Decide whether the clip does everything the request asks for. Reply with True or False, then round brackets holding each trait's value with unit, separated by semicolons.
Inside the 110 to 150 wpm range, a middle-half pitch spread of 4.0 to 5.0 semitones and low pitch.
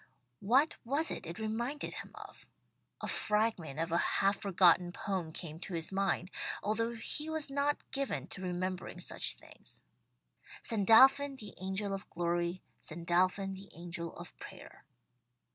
False (145 wpm; 4.6 semitones; 195 Hz)